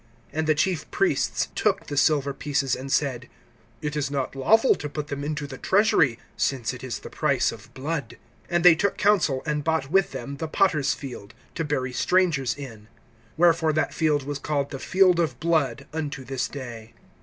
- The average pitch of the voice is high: No, medium, 145 Hz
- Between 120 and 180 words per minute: No, average, 190 wpm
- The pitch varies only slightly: No, average, 3.3 semitones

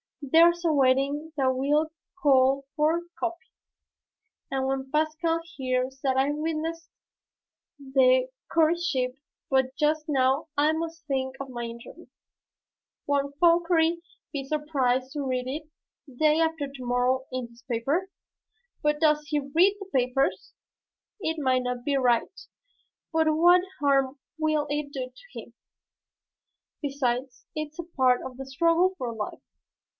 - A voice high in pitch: Yes, very high, 285 Hz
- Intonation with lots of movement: No, average, 3.5 semitones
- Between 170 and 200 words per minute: No, slow, 135 wpm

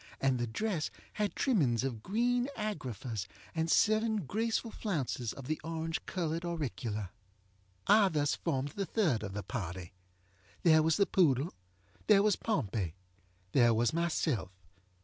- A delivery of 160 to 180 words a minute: No, average, 140 wpm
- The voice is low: No, medium, 155 Hz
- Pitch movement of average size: No, wide, 8.9 semitones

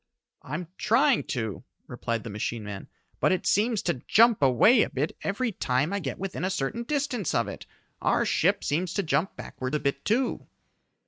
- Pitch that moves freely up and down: Yes, wide, 9.0 semitones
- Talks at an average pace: Yes, average, 185 wpm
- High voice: No, medium, 175 Hz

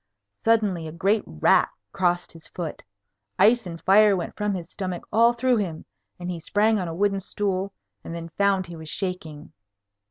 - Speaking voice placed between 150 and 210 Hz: Yes, medium, 185 Hz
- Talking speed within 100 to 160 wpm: No, average, 180 wpm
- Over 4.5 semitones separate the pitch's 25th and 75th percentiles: No, average, 3.5 semitones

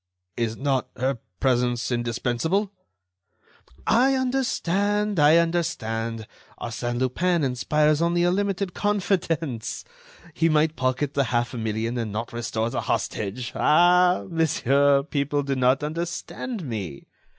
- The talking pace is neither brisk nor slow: No, slow, 115 wpm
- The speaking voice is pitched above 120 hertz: Yes, medium, 140 Hz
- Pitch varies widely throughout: Yes, wide, 6.4 semitones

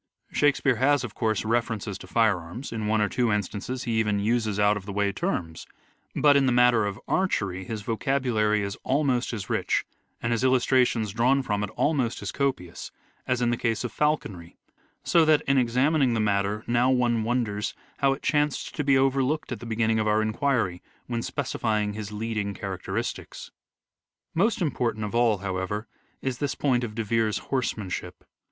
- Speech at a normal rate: Yes, average, 180 wpm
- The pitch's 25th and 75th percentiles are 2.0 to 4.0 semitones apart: Yes, average, 3.7 semitones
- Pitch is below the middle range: Yes, low, 115 Hz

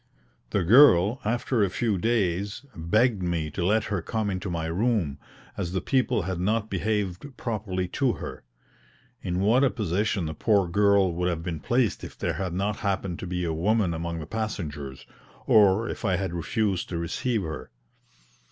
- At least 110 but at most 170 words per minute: No, average, 180 wpm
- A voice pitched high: No, very low, 95 Hz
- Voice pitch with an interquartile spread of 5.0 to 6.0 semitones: No, average, 4.1 semitones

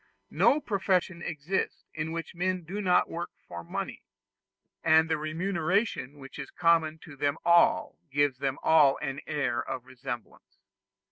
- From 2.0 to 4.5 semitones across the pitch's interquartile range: Yes, average, 3.8 semitones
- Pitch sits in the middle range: Yes, medium, 160 Hz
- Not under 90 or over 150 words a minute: Yes, average, 145 wpm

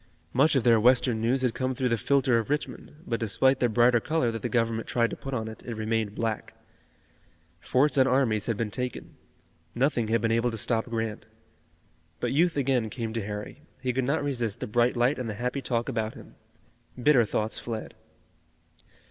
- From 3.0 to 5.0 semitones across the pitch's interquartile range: No, narrow, 2.6 semitones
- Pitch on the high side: No, low, 120 Hz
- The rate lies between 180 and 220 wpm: Yes, average, 200 wpm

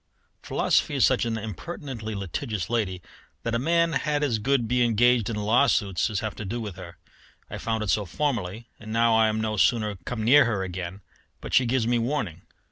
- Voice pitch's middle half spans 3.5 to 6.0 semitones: No, average, 2.9 semitones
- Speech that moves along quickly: Yes, fast, 210 wpm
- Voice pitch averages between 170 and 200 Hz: No, low, 110 Hz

